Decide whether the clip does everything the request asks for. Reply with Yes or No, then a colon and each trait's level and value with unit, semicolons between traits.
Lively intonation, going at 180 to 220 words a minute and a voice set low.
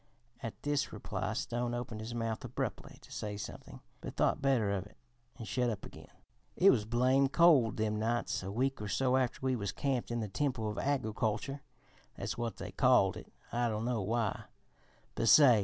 No: average, 3.4 semitones; average, 190 wpm; low, 120 Hz